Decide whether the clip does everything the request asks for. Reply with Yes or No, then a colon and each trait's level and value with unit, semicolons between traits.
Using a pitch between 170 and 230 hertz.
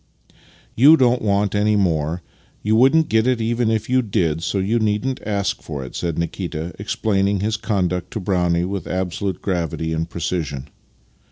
No: low, 100 Hz